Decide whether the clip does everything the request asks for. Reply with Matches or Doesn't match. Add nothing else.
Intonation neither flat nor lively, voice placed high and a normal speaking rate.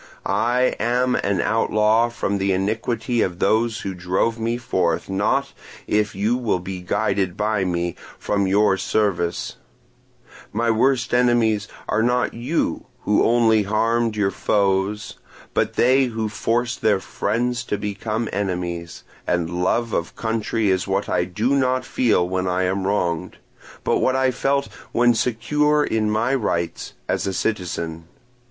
Doesn't match